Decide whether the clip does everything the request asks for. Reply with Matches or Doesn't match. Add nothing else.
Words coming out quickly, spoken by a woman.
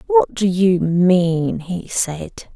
Doesn't match